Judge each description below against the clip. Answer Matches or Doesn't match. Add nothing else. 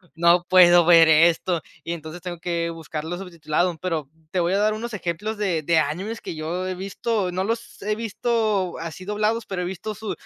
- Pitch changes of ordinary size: Matches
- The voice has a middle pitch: Matches